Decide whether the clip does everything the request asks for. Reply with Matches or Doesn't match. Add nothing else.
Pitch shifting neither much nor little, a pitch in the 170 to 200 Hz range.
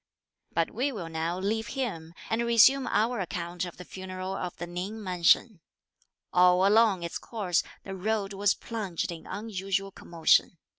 Matches